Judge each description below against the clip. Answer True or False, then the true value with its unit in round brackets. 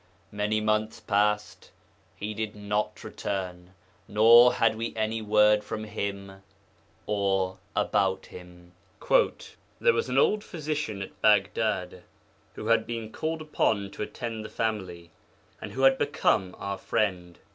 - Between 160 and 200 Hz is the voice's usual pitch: False (105 Hz)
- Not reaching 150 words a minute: True (135 wpm)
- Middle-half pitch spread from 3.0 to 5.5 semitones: False (2.5 semitones)